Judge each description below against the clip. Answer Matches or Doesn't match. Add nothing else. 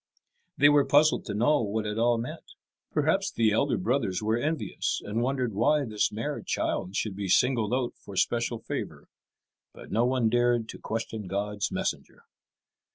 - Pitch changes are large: Doesn't match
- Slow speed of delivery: Doesn't match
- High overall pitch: Doesn't match